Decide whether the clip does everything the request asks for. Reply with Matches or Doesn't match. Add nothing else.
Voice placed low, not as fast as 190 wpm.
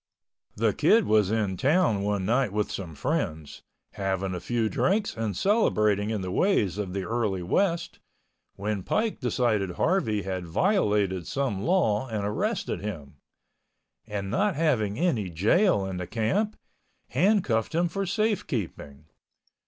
Matches